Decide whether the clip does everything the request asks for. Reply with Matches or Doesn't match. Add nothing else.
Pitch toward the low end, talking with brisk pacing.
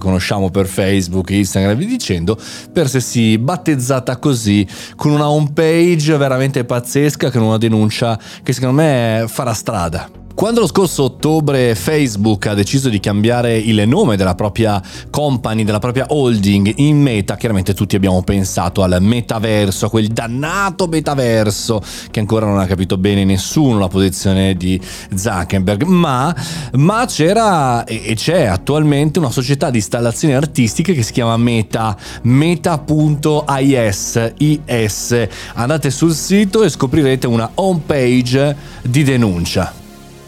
Doesn't match